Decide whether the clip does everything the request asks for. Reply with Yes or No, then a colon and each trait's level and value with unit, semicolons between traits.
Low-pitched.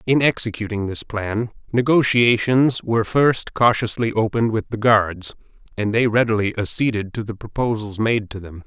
Yes: low, 110 Hz